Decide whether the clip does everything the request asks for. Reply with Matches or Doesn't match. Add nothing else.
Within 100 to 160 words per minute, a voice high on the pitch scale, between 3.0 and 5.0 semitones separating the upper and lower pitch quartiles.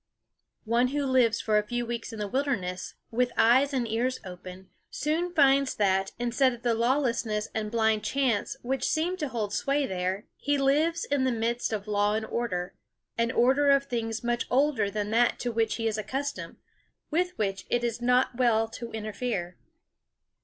Doesn't match